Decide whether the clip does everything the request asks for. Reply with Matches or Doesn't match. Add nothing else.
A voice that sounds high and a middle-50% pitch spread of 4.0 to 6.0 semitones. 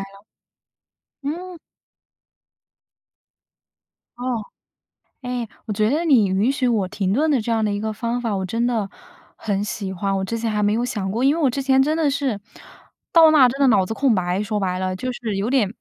Matches